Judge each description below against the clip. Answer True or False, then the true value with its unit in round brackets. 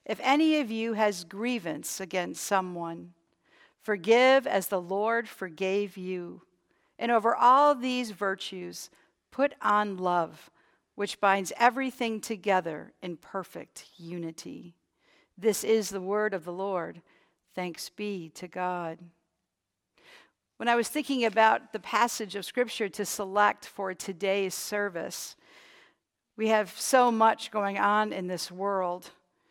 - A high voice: True (200 Hz)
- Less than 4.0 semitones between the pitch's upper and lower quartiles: True (3.4 semitones)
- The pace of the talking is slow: True (130 wpm)